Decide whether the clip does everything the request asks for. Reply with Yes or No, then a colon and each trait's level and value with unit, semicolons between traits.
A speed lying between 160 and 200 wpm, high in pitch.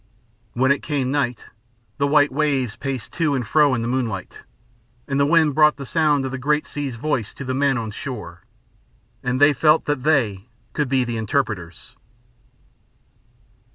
No: average, 170 wpm; low, 135 Hz